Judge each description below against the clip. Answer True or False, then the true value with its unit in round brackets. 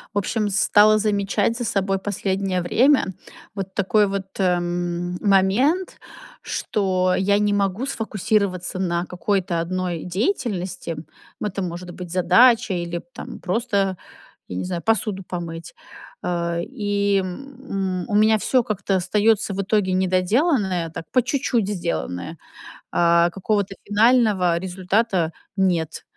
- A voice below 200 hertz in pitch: True (190 Hz)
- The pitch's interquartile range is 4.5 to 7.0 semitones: False (2.9 semitones)